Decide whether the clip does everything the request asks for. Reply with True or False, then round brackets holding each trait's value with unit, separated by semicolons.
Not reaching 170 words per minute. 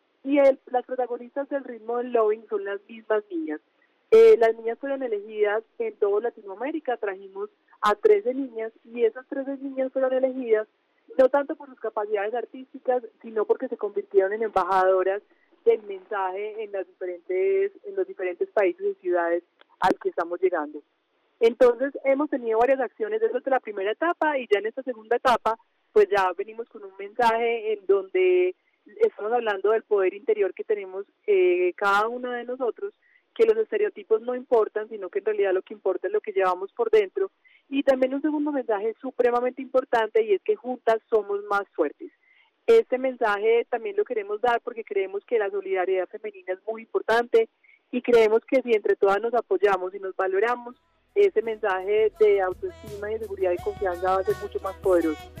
False (180 wpm)